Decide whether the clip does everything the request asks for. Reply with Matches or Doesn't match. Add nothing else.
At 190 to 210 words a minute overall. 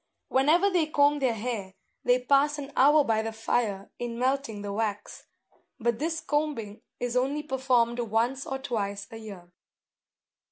Doesn't match